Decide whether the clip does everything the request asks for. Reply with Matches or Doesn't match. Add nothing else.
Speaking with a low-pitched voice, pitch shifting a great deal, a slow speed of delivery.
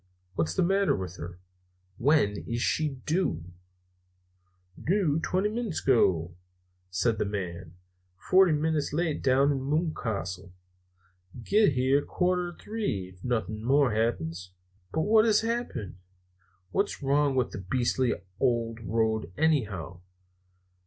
Matches